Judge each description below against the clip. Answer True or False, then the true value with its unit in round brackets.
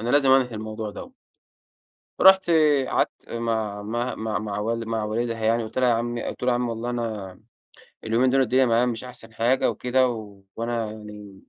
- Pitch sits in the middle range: False (115 Hz)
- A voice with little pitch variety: True (2.2 semitones)